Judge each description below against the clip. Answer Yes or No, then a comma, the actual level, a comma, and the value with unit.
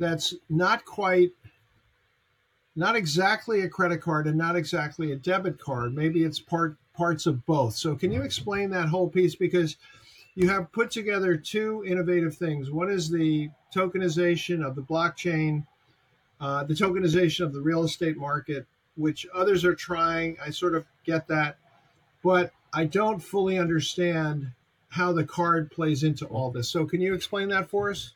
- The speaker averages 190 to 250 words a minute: No, average, 165 wpm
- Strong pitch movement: No, average, 3.1 semitones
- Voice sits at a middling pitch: Yes, medium, 165 Hz